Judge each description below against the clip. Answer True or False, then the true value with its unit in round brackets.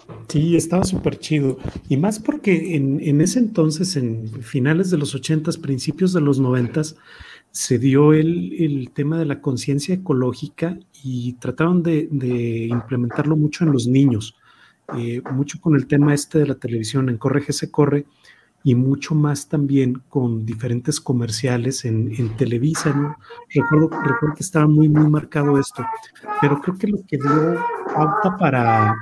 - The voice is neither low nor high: True (145 Hz)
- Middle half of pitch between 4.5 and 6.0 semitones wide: False (3.5 semitones)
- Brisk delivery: False (160 wpm)